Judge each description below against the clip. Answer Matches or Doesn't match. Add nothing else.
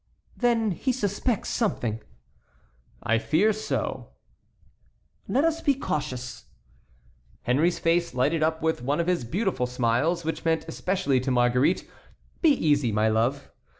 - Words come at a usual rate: Doesn't match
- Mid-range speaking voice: Matches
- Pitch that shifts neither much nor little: Doesn't match